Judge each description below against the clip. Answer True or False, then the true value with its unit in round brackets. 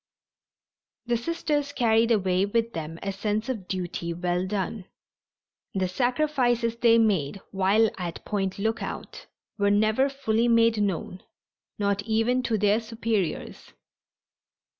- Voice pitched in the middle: False (215 Hz)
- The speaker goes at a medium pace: False (120 wpm)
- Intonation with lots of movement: False (3.3 semitones)